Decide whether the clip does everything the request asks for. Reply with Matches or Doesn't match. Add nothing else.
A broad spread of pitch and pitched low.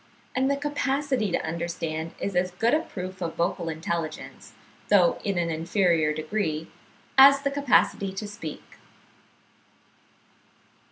Doesn't match